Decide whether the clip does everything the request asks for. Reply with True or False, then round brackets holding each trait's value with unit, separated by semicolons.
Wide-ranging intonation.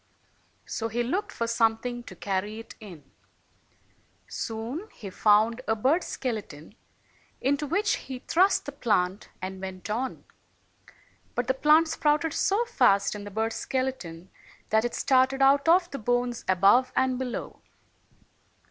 False (4.7 semitones)